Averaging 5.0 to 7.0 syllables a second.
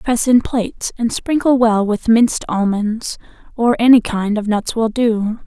No: 4.3 syllables/s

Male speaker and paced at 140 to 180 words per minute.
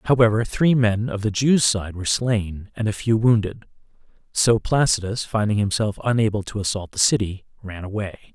Yes: male; average, 175 wpm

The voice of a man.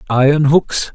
Yes: male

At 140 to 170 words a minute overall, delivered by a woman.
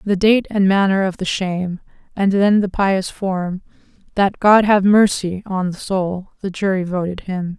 No: average, 180 wpm; female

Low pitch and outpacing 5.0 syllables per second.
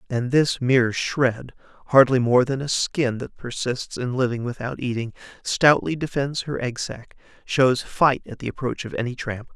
No: low, 125 Hz; 4.6 syllables/s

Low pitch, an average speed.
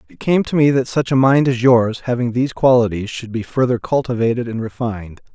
No: low, 120 Hz; fast, 215 wpm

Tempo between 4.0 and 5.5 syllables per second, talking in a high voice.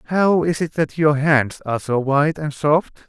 No: 4.6 syllables/s; medium, 150 Hz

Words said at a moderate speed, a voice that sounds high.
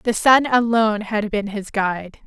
Yes: average, 185 wpm; high, 215 Hz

